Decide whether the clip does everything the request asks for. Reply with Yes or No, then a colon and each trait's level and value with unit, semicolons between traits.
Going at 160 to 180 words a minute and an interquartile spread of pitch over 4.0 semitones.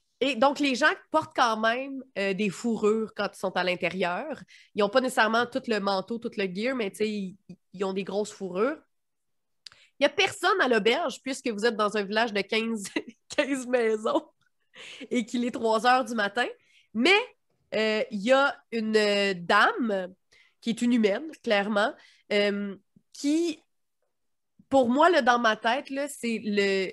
Yes: average, 175 wpm; average, 4.7 semitones